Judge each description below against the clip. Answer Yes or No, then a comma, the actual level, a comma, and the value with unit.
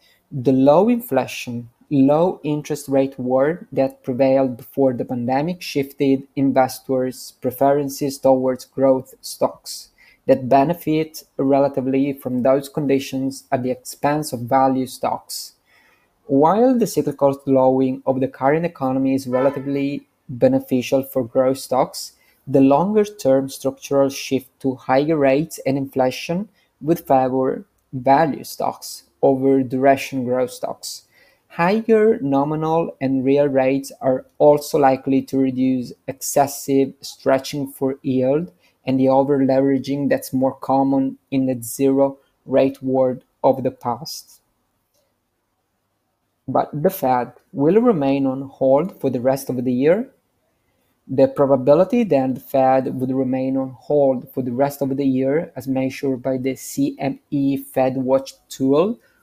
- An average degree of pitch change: No, narrow, 1.1 semitones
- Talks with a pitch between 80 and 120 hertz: No, low, 135 Hz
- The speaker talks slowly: Yes, slow, 125 wpm